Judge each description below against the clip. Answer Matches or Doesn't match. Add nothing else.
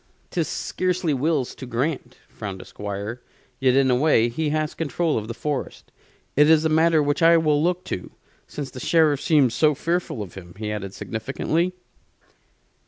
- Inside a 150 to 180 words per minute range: Matches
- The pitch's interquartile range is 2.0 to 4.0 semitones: Doesn't match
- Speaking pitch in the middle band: Matches